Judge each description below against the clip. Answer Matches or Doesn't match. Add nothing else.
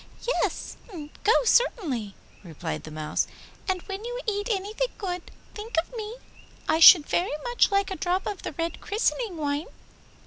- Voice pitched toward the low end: Doesn't match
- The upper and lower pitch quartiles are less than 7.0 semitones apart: Matches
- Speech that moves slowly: Doesn't match